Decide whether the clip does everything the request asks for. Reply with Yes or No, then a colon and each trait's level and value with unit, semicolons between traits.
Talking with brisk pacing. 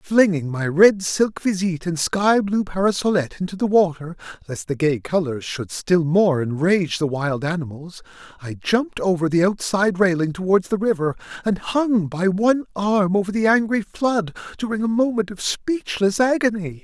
No: average, 170 wpm